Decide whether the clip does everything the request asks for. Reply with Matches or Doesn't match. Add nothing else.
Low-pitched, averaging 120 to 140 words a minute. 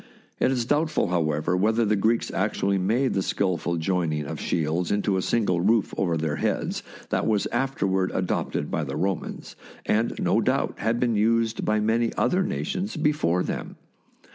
Doesn't match